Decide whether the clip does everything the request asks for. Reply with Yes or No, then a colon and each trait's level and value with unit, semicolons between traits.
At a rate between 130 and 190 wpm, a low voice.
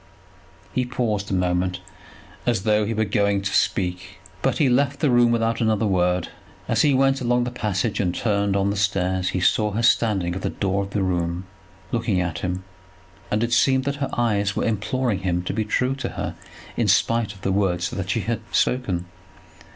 No: average, 200 wpm; low, 105 Hz